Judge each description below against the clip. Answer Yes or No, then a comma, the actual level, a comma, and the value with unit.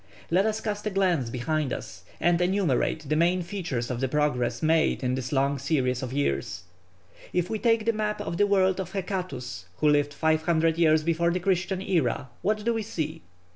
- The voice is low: No, medium, 165 Hz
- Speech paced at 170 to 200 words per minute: Yes, average, 195 wpm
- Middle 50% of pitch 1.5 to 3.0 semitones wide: No, wide, 5.4 semitones